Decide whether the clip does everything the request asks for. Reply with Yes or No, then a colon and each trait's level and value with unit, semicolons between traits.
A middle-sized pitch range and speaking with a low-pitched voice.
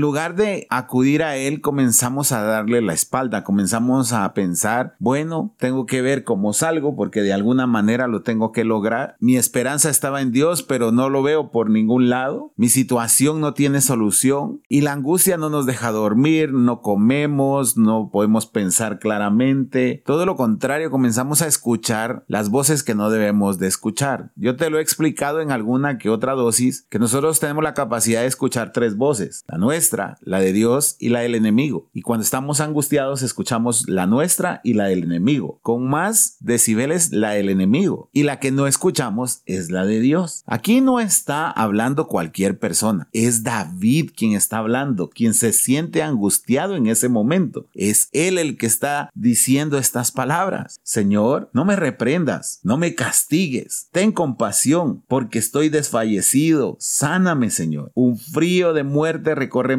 Yes: average, 4.7 semitones; low, 130 Hz